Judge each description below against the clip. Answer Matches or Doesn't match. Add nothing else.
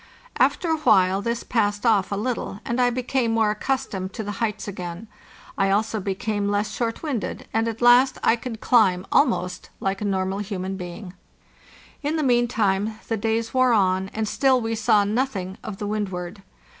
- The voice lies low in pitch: Doesn't match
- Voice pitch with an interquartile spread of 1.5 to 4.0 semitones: Matches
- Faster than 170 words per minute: Matches